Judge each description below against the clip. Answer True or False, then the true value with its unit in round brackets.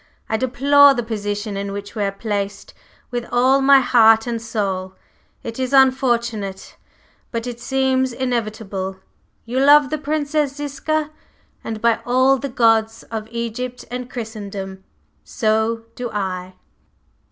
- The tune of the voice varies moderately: True (3.8 semitones)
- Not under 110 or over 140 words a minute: True (135 wpm)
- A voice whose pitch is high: True (235 Hz)